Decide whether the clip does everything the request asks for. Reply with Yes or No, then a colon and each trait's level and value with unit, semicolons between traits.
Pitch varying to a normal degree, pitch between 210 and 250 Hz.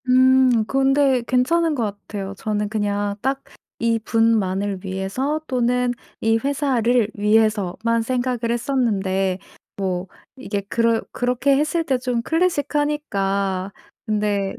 Yes: average, 4.4 semitones; high, 230 Hz